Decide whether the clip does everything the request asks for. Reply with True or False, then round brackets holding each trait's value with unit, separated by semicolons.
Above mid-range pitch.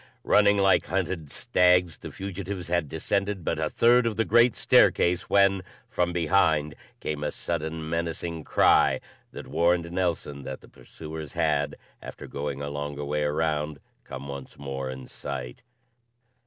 False (80 Hz)